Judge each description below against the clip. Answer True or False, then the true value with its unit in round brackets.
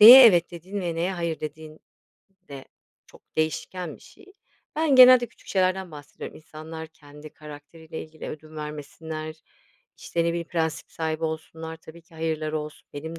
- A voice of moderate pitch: True (160 Hz)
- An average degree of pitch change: False (1.8 semitones)